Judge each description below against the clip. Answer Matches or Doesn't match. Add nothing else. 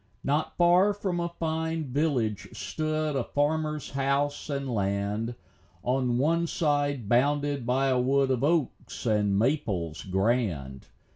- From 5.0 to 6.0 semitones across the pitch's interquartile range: Matches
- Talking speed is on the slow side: Matches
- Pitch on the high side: Doesn't match